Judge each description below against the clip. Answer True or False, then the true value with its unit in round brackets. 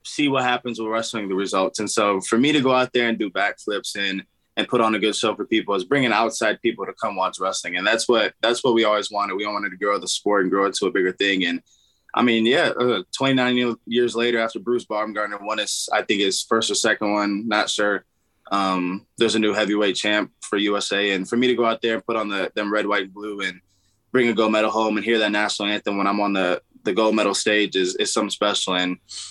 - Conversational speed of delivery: False (260 wpm)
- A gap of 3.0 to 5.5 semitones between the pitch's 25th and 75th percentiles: False (2.5 semitones)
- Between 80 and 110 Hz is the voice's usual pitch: True (105 Hz)